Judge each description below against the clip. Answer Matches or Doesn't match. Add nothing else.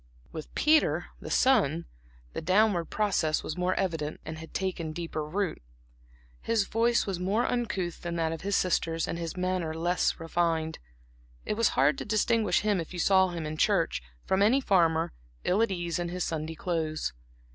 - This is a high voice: Doesn't match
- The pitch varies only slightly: Doesn't match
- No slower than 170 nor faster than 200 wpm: Matches